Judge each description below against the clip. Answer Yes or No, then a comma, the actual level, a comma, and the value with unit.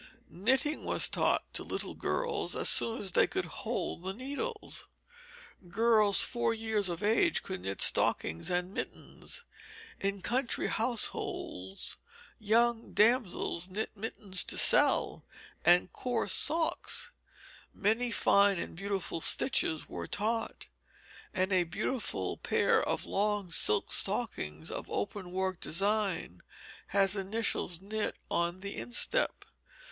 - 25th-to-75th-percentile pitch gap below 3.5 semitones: No, average, 4.2 semitones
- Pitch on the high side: Yes, high, 205 Hz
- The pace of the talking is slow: Yes, slow, 120 wpm